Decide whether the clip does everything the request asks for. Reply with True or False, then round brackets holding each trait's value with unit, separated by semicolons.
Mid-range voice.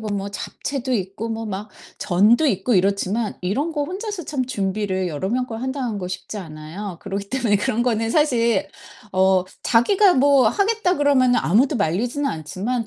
False (225 Hz)